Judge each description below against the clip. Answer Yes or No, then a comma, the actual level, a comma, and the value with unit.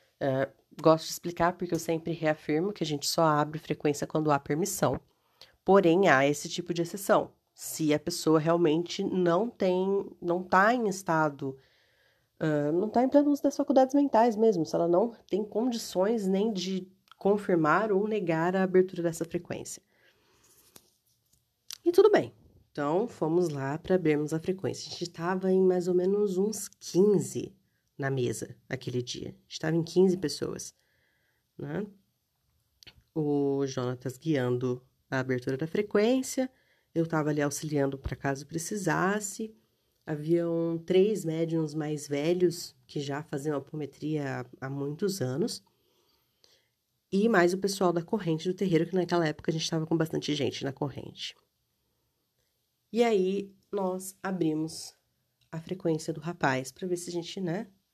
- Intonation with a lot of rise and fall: No, average, 4.2 semitones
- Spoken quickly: No, average, 155 wpm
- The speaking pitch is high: No, medium, 170 Hz